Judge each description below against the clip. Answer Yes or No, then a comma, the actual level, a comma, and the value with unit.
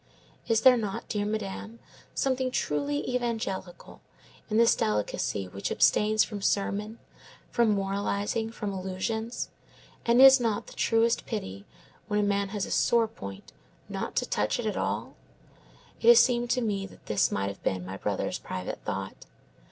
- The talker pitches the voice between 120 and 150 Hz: No, high, 210 Hz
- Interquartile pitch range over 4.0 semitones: No, average, 3.7 semitones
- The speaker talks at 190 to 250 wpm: No, average, 160 wpm